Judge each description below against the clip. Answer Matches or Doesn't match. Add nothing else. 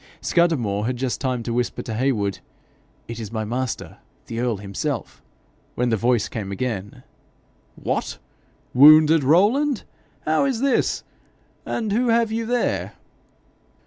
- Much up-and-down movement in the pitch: Matches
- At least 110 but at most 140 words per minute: Matches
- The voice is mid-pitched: Doesn't match